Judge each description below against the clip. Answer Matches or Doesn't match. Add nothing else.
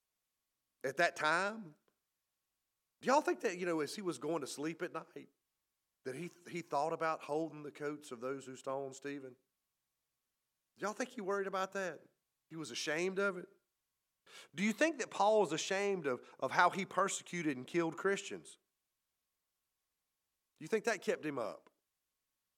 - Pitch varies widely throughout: Doesn't match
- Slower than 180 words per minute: Matches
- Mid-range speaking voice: Matches